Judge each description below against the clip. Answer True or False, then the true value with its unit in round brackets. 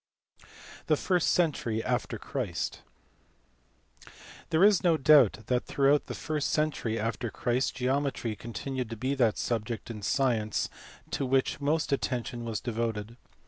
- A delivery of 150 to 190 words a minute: False (135 wpm)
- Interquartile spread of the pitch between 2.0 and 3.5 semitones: False (4.0 semitones)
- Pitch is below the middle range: True (125 Hz)